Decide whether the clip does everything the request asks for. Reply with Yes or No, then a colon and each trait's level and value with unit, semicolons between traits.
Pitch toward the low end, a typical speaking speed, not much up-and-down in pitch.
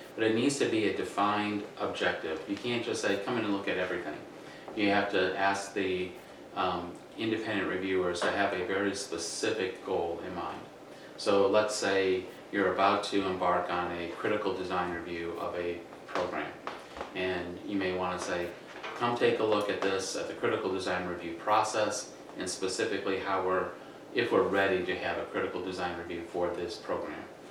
Yes: very low, 95 Hz; average, 180 wpm; narrow, 2.3 semitones